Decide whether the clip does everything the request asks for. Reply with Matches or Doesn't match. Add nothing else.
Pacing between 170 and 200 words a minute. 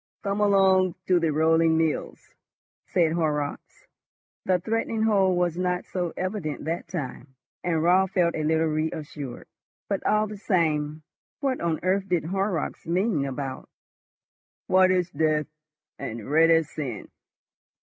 Doesn't match